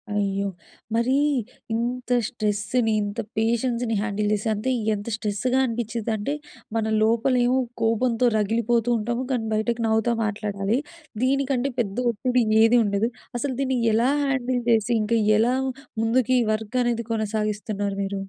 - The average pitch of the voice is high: Yes, high, 230 Hz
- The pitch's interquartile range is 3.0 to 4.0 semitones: No, narrow, 2.6 semitones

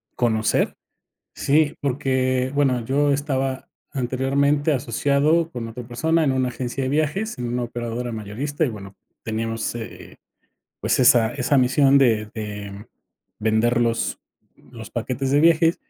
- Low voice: Yes, low, 130 Hz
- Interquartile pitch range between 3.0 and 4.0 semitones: Yes, average, 3.5 semitones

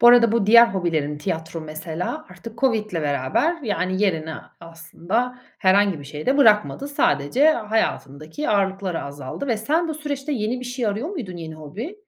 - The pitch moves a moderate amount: No, wide, 7.5 semitones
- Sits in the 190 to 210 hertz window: Yes, high, 205 Hz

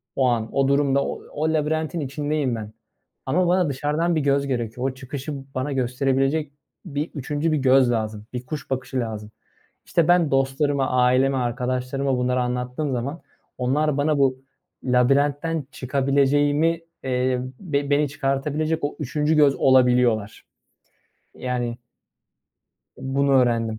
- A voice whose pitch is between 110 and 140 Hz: Yes, low, 135 Hz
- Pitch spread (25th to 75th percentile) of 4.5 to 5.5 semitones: No, average, 2.8 semitones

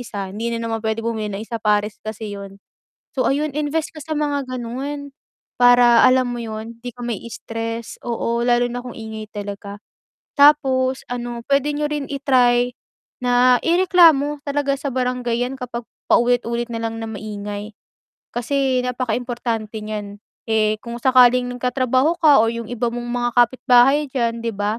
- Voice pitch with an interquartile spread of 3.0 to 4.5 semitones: No, narrow, 2.5 semitones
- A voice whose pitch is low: No, high, 240 Hz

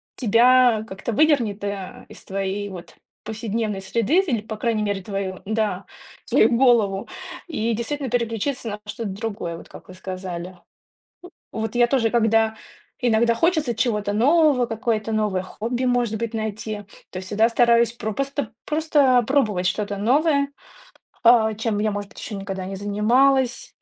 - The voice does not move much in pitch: No, average, 3.2 semitones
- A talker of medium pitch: No, high, 220 Hz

